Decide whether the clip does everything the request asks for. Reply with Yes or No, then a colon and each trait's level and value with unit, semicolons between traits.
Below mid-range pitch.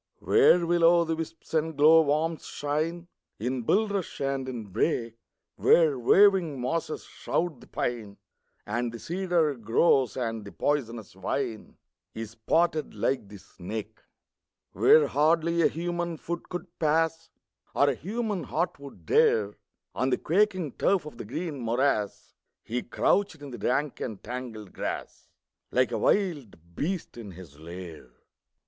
No: medium, 145 Hz